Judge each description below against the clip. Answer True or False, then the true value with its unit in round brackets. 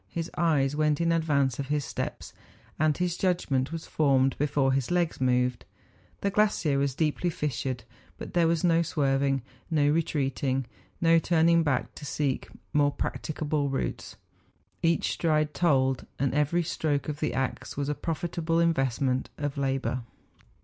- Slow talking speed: False (155 wpm)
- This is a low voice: False (150 Hz)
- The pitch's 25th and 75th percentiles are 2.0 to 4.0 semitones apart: True (3.4 semitones)